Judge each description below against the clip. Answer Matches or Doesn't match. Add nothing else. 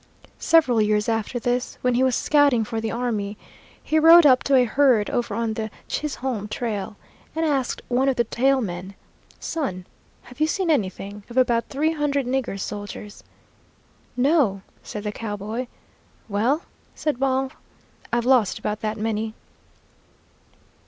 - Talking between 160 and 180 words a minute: Doesn't match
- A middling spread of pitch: Matches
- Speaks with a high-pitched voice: Matches